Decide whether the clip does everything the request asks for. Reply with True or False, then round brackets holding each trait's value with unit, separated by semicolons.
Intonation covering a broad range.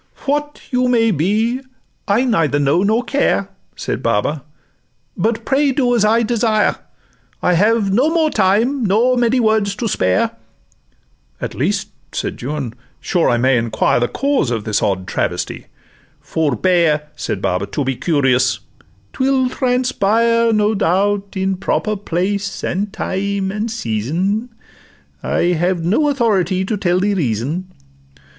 True (6.3 semitones)